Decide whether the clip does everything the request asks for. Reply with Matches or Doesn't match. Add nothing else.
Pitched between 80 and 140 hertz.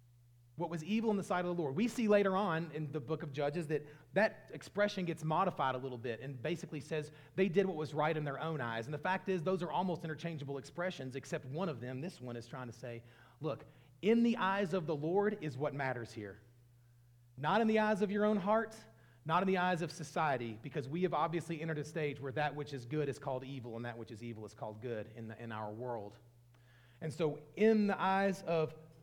Doesn't match